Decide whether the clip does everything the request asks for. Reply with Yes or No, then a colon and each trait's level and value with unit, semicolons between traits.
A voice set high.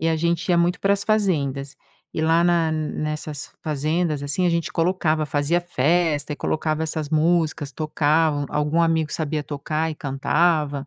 No: medium, 155 Hz